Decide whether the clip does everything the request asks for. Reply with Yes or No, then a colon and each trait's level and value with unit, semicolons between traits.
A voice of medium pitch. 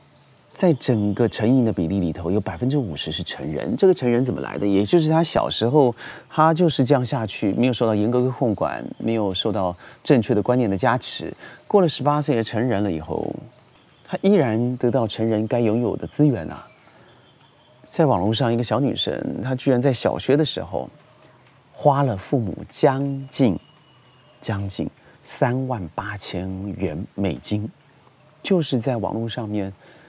No: low, 125 Hz